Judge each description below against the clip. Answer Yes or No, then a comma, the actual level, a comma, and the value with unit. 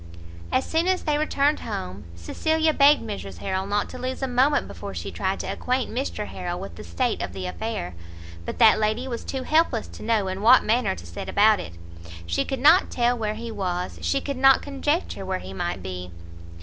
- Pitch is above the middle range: Yes, high, 225 Hz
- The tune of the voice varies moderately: No, wide, 7.0 semitones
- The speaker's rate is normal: No, fast, 210 wpm